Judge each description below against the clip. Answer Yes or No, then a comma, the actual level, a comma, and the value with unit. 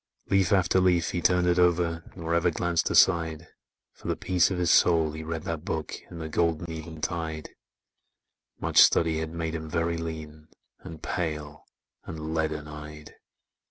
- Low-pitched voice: Yes, very low, 80 Hz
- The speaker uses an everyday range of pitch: No, narrow, 1.6 semitones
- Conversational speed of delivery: Yes, average, 160 wpm